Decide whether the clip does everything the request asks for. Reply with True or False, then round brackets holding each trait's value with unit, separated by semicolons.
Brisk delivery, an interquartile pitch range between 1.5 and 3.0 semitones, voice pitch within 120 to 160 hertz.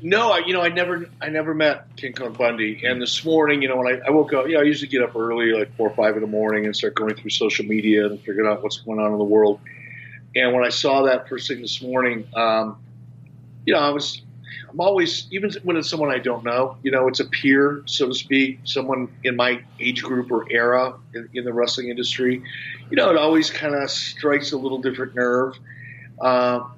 True (240 wpm; 2.4 semitones; 125 Hz)